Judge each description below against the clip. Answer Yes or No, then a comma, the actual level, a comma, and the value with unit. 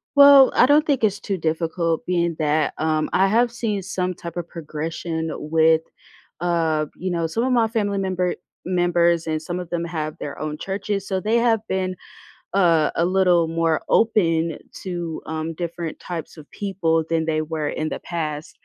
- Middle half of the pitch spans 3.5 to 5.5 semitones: No, average, 3.1 semitones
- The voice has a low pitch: No, medium, 170 Hz